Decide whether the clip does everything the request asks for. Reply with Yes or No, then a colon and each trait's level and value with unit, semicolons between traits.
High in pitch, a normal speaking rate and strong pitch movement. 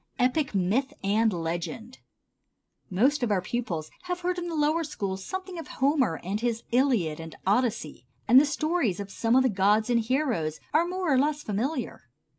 Yes: high, 240 Hz; average, 180 wpm; wide, 7.1 semitones